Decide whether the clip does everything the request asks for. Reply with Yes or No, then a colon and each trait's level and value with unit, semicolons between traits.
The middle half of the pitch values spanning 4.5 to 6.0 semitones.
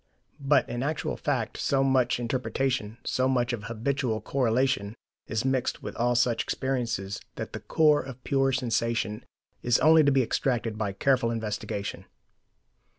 No: average, 2.9 semitones